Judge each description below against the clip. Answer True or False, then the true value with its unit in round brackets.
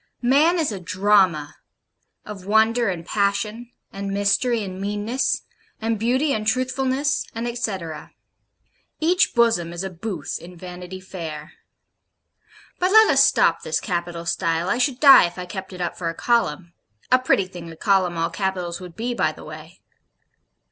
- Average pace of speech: True (160 wpm)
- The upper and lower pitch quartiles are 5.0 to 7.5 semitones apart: True (5.4 semitones)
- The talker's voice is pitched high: True (195 Hz)